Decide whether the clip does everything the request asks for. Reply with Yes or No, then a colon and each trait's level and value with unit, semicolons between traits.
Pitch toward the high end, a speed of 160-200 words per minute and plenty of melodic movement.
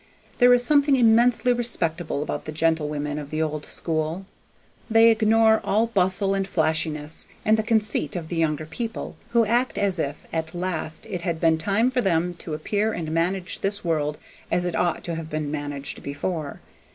No: medium, 175 Hz; average, 180 wpm; wide, 5.8 semitones